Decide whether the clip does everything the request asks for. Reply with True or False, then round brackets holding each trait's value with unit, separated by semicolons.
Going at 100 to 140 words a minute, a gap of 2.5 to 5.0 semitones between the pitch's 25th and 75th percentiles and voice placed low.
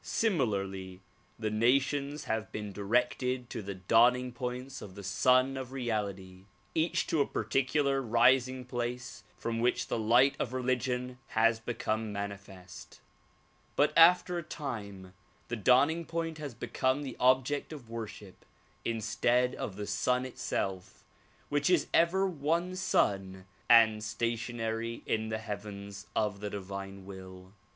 True (135 wpm; 4.3 semitones; 115 Hz)